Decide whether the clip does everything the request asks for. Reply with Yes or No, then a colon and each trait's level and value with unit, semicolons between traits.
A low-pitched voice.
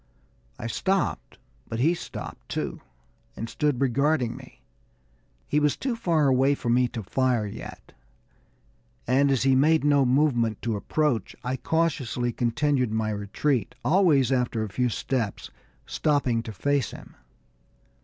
Yes: low, 130 Hz